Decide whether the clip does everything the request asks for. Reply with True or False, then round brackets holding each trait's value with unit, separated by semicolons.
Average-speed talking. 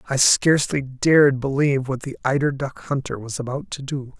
True (185 wpm)